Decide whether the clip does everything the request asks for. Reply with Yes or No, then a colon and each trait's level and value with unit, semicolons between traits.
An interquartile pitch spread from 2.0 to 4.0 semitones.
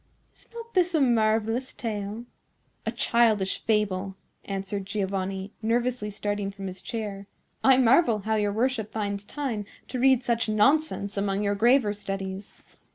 Yes: average, 3.2 semitones